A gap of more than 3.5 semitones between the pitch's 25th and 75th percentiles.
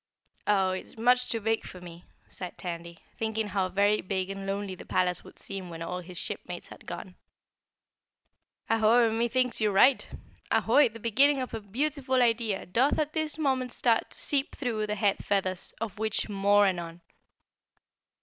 Yes: average, 4.4 semitones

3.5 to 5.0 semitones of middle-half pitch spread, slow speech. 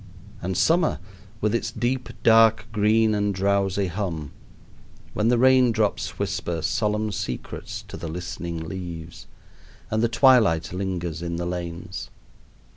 Yes: average, 4.6 semitones; slow, 130 wpm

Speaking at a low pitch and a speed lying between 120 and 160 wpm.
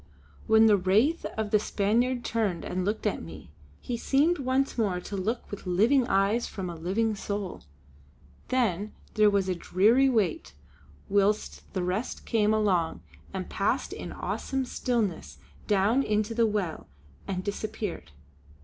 No: high, 210 Hz; average, 150 wpm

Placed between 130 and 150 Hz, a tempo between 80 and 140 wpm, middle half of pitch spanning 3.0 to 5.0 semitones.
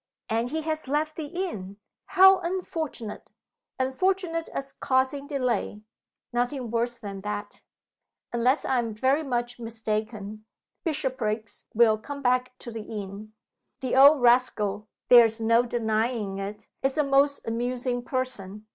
No: high, 245 Hz; slow, 135 wpm; average, 4.2 semitones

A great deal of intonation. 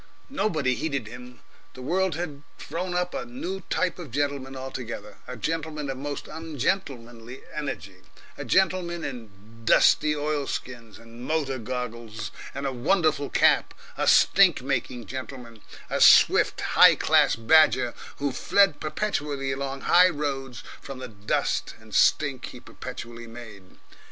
No: average, 4.8 semitones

